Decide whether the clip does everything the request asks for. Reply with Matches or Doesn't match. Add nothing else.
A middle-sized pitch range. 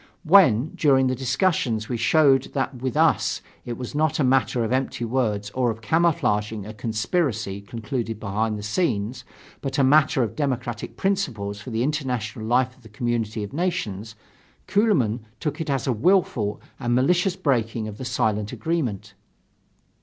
Matches